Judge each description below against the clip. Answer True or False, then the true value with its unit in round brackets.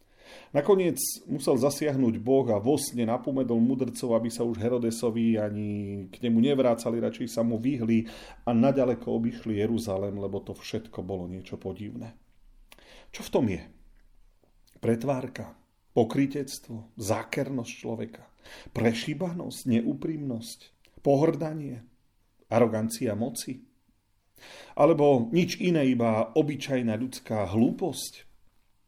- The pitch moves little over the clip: False (3.2 semitones)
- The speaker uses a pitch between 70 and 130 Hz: True (115 Hz)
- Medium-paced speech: False (105 wpm)